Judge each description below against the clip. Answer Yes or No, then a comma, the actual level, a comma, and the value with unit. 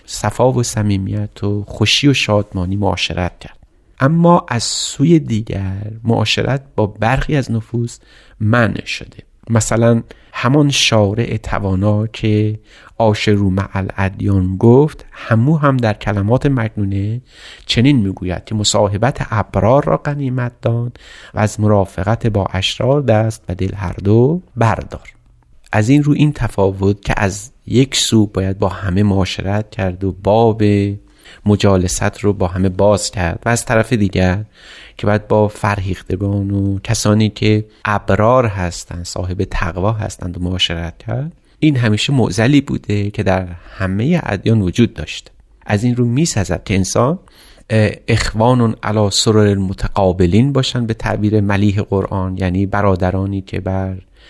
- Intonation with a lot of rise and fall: No, average, 3.2 semitones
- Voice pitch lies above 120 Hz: No, low, 105 Hz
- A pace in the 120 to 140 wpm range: Yes, average, 135 wpm